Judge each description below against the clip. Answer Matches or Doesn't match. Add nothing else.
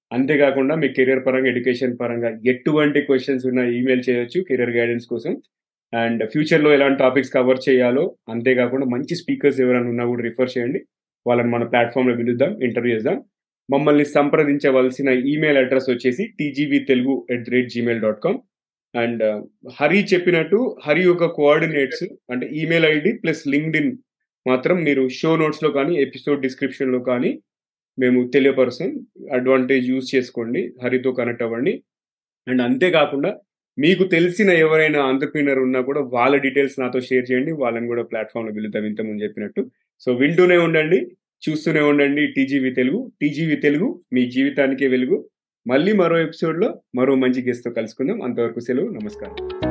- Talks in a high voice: Doesn't match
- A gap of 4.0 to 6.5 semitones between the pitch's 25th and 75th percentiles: Doesn't match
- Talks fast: Matches